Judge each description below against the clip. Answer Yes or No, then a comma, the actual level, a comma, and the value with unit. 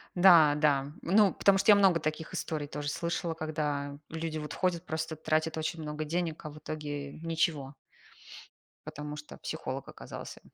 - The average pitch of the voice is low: No, medium, 155 Hz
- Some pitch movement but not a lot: No, narrow, 2.0 semitones